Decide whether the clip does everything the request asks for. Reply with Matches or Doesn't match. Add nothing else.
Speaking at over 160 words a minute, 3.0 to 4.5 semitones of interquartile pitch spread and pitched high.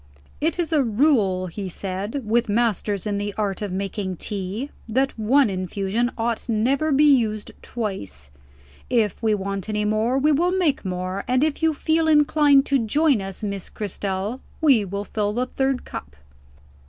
Doesn't match